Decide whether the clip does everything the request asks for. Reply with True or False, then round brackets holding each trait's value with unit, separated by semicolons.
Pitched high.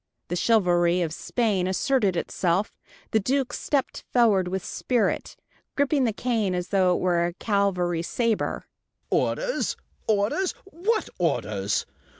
True (200 Hz)